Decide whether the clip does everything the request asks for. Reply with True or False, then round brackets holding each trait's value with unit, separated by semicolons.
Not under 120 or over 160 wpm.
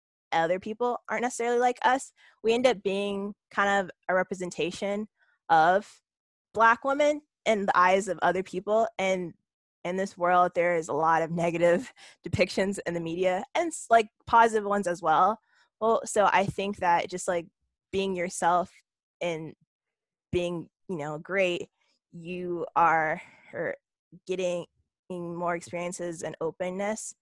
True (140 wpm)